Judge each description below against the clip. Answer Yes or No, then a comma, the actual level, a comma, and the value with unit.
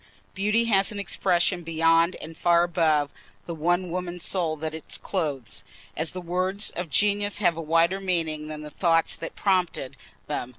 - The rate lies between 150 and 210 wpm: Yes, average, 170 wpm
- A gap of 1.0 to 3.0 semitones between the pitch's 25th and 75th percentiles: Yes, narrow, 2.6 semitones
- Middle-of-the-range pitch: Yes, medium, 170 Hz